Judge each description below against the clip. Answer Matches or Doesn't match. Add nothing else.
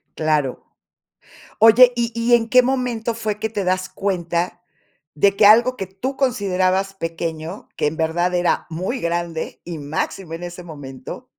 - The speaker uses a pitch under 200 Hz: Matches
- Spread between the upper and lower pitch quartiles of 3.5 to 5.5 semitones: Matches